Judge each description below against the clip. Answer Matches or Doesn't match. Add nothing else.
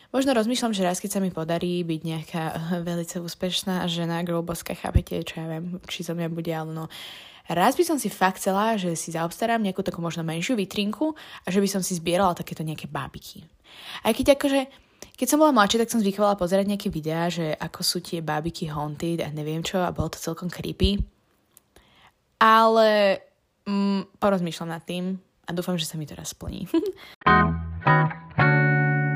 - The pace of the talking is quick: Matches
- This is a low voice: Doesn't match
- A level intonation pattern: Doesn't match